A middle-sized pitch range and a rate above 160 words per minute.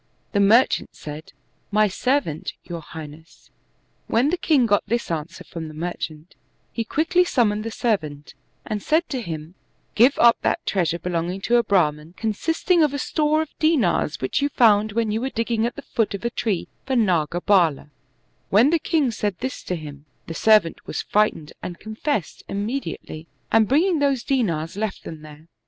No: wide, 7.0 semitones; average, 180 wpm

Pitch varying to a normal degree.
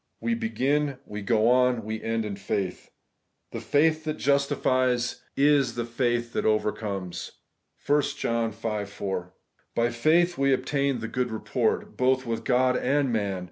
Yes: average, 4.0 semitones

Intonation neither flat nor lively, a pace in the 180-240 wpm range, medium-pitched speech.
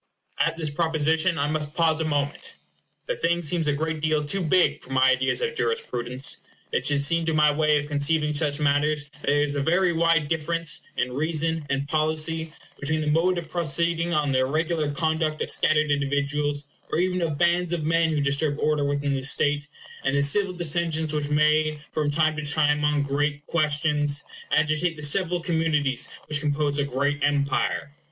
No: narrow, 2.1 semitones; average, 190 wpm; medium, 150 Hz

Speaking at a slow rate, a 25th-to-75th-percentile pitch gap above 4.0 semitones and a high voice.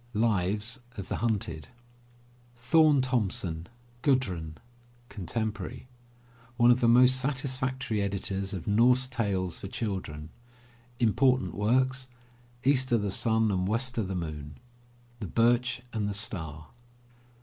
No: slow, 120 wpm; average, 4.9 semitones; low, 110 Hz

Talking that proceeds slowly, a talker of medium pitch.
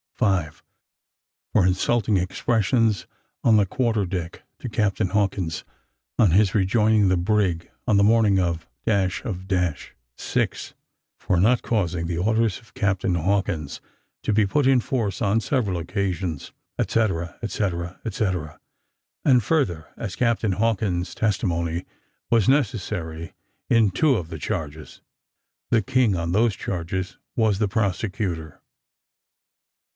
No: slow, 125 wpm; low, 100 Hz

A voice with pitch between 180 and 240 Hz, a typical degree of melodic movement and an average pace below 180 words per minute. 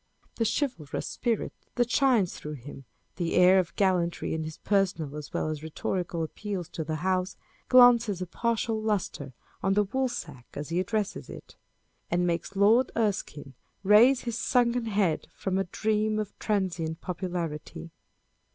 Yes: high, 190 Hz; average, 4.9 semitones; average, 150 wpm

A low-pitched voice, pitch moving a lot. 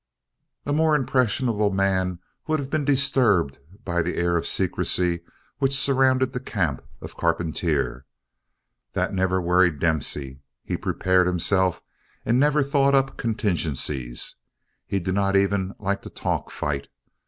Yes: very low, 95 Hz; wide, 7.2 semitones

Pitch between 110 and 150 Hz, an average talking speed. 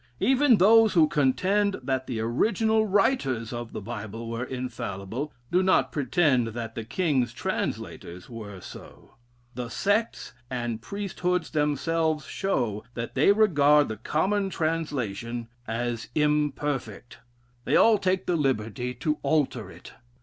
No: medium, 140 Hz; slow, 130 wpm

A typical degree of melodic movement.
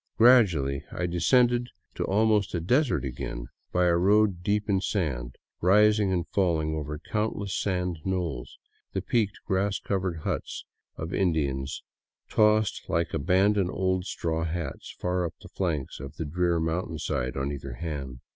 Yes: average, 4.5 semitones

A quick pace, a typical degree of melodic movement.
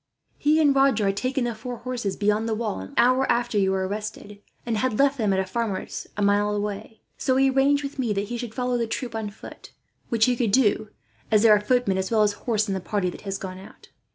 Yes: fast, 250 wpm; average, 3.6 semitones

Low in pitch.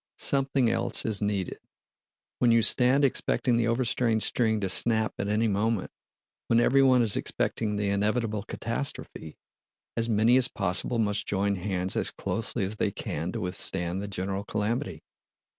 Yes: low, 110 Hz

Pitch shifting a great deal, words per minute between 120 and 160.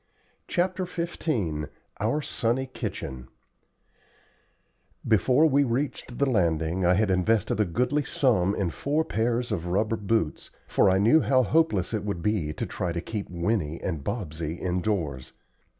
Yes: wide, 6.3 semitones; average, 145 wpm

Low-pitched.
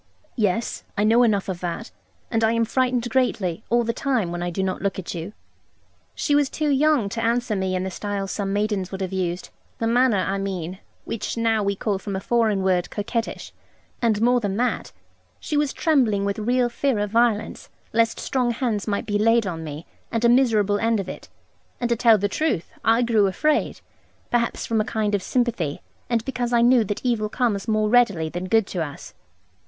No: high, 220 Hz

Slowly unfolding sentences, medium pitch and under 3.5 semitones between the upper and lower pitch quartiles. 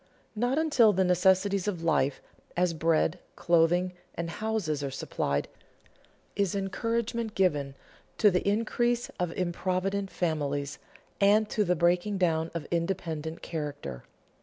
No: slow, 125 wpm; medium, 180 Hz; average, 3.9 semitones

